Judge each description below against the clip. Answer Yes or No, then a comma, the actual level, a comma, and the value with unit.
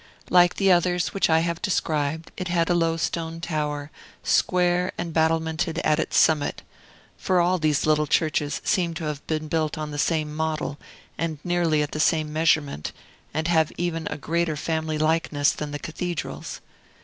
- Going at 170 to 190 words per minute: Yes, average, 175 wpm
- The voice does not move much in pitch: Yes, narrow, 2.0 semitones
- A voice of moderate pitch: Yes, medium, 160 Hz